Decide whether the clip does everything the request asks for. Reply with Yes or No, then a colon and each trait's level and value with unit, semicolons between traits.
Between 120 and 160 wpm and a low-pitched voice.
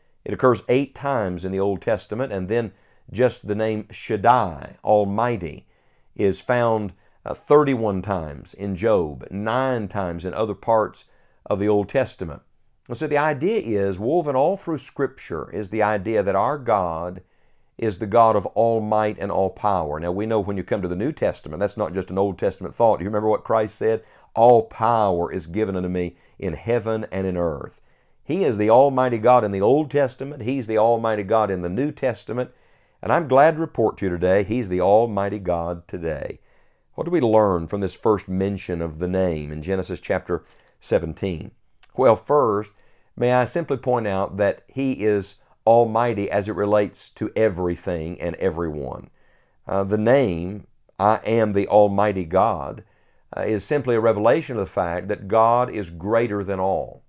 No: average, 180 wpm; low, 105 Hz